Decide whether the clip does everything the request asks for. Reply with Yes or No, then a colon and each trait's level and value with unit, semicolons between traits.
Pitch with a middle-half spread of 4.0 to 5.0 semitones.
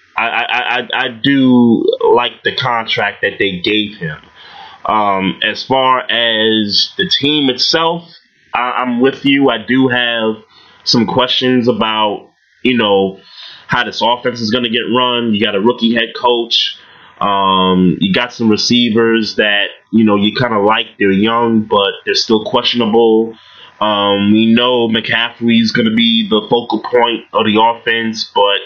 No: average, 2.8 semitones